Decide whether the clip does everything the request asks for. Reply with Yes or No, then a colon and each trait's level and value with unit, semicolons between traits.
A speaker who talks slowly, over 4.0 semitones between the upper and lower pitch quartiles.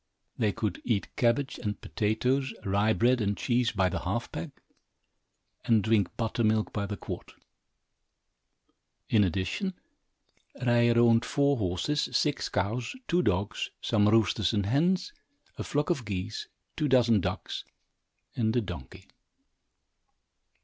No: slow, 130 wpm; average, 3.5 semitones